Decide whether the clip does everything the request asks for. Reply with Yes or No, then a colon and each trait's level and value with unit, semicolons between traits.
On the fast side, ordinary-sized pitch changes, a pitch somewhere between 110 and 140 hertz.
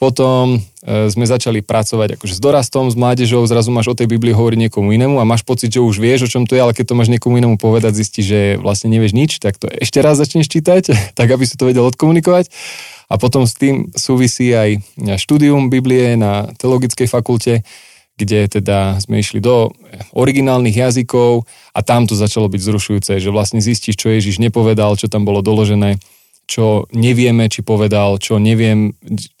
Yes: fast, 190 wpm; average, 3.0 semitones; low, 115 Hz